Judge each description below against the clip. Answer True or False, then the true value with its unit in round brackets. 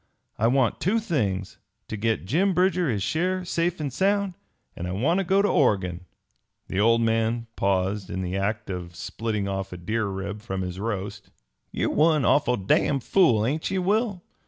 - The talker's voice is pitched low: True (115 Hz)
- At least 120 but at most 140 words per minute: False (180 wpm)